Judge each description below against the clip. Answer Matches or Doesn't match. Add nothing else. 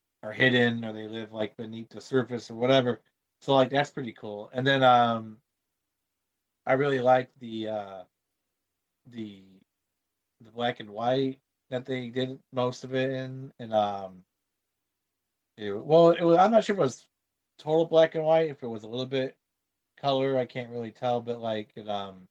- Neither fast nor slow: Matches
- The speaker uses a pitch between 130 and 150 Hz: Doesn't match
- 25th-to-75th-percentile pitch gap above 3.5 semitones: Matches